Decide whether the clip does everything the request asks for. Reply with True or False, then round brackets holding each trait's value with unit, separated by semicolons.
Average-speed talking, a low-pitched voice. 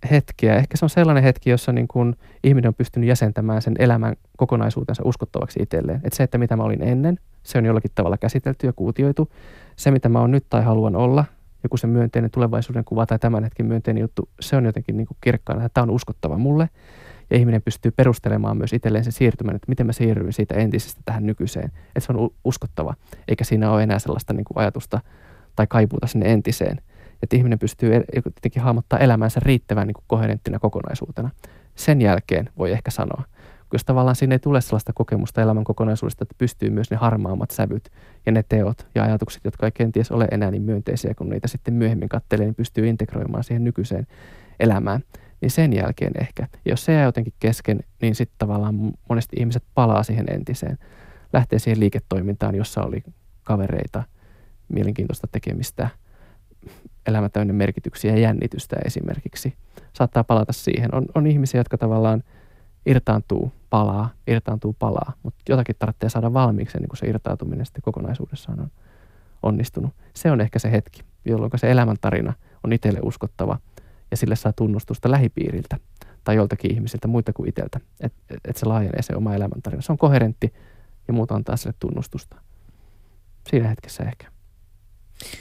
False (170 wpm; 115 Hz)